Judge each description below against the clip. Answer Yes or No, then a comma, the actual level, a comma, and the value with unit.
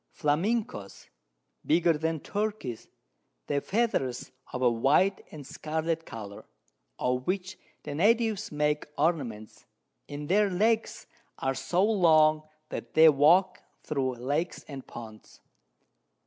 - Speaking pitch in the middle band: Yes, medium, 155 Hz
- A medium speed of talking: No, slow, 115 wpm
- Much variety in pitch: Yes, wide, 5.9 semitones